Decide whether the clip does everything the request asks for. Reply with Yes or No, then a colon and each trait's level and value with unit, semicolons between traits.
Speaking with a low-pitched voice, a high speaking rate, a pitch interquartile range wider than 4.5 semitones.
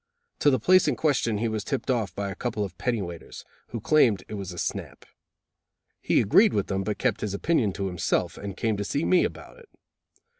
Yes: low, 105 Hz; fast, 220 wpm; average, 5.1 semitones